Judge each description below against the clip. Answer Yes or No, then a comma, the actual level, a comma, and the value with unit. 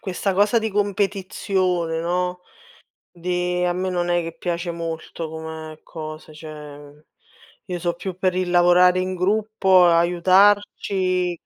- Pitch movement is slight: Yes, narrow, 2.0 semitones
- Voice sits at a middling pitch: Yes, medium, 180 Hz